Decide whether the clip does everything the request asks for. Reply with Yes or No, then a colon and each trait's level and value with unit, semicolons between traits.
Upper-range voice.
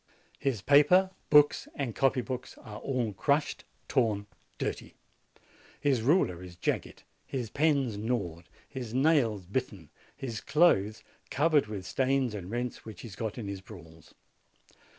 No: low, 120 Hz